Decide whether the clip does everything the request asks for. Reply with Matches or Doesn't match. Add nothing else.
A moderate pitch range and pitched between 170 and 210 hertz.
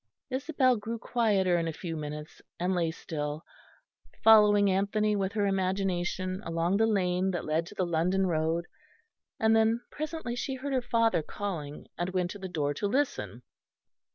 Matches